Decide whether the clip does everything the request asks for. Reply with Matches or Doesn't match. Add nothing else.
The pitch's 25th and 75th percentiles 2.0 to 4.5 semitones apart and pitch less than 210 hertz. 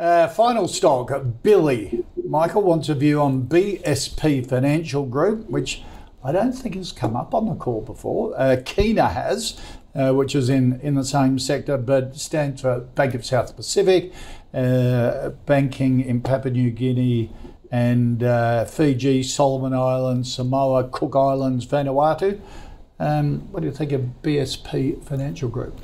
Matches